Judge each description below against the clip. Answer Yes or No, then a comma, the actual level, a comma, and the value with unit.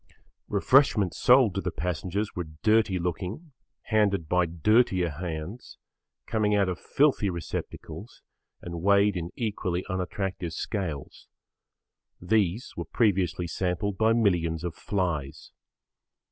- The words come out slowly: Yes, slow, 115 wpm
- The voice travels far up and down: No, average, 3.6 semitones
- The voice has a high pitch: No, very low, 95 Hz